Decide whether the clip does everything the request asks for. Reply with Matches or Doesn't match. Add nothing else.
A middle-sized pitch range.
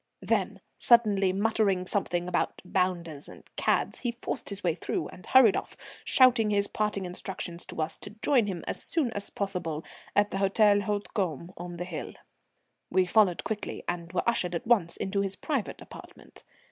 Matches